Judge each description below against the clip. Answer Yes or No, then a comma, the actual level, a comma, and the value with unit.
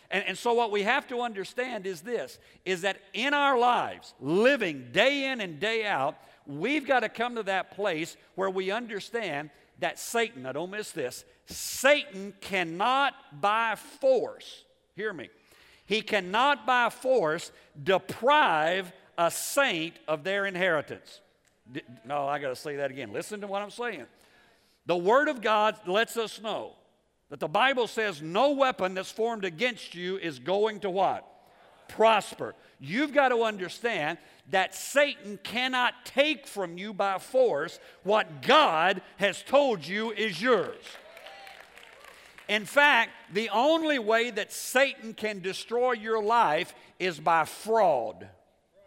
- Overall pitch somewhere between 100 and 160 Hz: No, high, 215 Hz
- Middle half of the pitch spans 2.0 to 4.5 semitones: No, average, 5.1 semitones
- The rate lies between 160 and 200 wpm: No, average, 145 wpm